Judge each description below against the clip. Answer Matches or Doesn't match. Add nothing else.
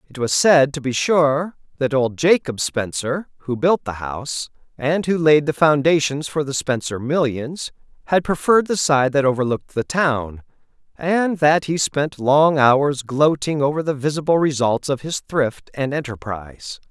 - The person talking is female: Doesn't match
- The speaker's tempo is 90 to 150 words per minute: Doesn't match